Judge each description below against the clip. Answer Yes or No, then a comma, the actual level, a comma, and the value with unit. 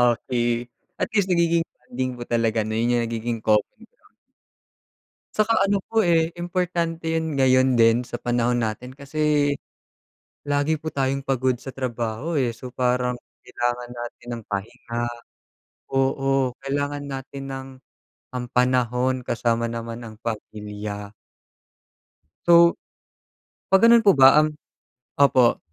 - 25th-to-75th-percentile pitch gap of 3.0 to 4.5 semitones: Yes, average, 3.6 semitones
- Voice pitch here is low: Yes, low, 130 Hz